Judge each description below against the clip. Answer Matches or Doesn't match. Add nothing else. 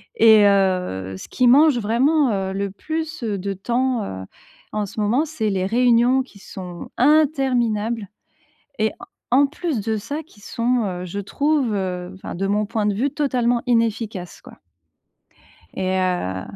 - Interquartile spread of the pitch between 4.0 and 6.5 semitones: Matches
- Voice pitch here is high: Matches